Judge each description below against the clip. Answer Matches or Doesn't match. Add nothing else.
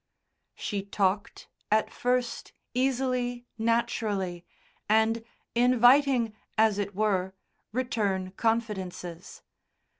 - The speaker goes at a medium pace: Doesn't match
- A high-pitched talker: Matches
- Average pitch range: Matches